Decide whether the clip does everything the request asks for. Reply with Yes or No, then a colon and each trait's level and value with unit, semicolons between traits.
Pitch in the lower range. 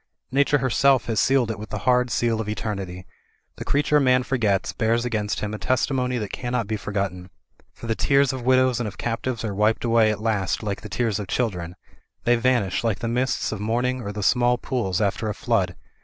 Yes: low, 115 Hz